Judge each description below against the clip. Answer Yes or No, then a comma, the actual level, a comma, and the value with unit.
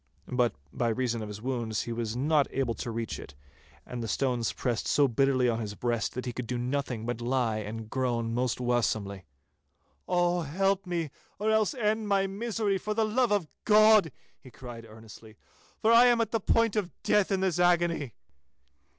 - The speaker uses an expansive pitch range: Yes, wide, 8.8 semitones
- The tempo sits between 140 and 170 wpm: No, average, 185 wpm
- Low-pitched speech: Yes, low, 130 Hz